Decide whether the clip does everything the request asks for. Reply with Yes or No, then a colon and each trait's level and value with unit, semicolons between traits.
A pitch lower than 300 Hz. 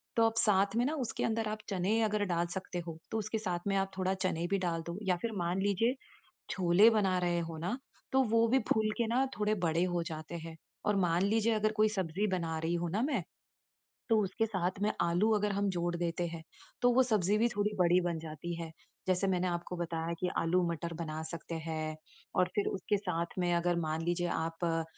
Yes: medium, 185 Hz